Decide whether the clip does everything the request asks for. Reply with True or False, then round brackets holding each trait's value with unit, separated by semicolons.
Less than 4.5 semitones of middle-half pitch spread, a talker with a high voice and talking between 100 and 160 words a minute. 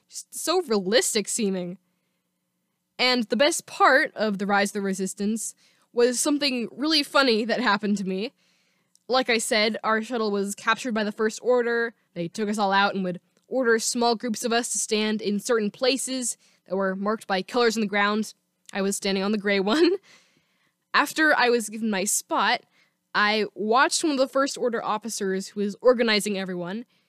False (3.5 semitones; 215 Hz; 185 wpm)